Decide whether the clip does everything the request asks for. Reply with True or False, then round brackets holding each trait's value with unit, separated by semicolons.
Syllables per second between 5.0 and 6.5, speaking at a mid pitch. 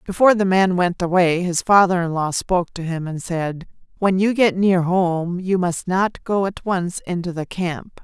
False (4.5 syllables/s; 180 Hz)